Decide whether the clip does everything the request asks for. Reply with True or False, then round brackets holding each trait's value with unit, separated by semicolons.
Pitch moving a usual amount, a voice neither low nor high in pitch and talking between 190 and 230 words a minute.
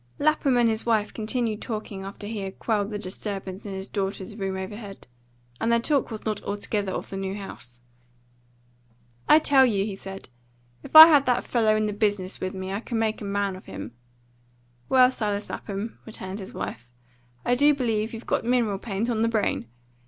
False (3.0 semitones; 210 Hz; 195 wpm)